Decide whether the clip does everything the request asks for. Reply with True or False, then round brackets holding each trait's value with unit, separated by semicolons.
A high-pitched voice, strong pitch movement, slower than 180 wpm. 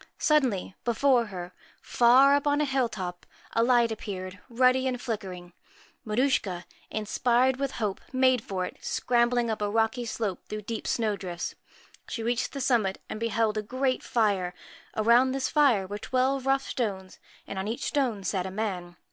False (230 Hz; 4.4 semitones; 170 wpm)